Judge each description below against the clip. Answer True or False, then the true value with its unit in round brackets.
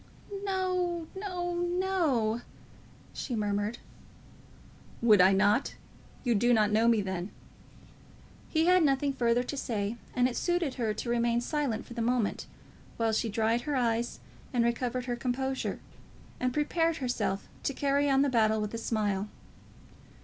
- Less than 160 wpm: True (150 wpm)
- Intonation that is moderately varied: True (4.5 semitones)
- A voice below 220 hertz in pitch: False (245 Hz)